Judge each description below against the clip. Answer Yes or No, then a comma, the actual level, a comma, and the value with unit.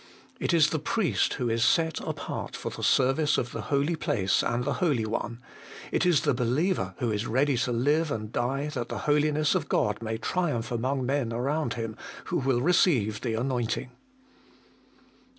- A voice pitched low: Yes, low, 130 Hz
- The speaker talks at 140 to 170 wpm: No, average, 180 wpm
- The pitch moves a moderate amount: Yes, average, 4.3 semitones